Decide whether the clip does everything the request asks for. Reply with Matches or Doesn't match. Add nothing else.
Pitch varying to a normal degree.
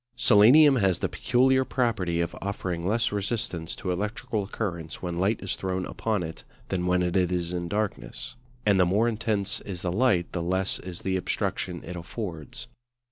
Matches